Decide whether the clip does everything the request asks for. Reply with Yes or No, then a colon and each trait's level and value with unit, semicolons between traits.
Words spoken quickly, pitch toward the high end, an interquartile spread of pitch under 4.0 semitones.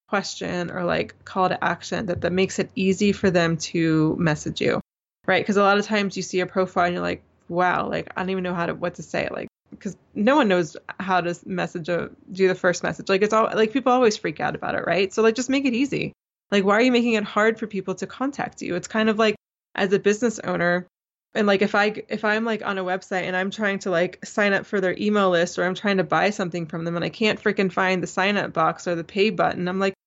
Yes: fast, 265 wpm; high, 195 Hz; average, 2.8 semitones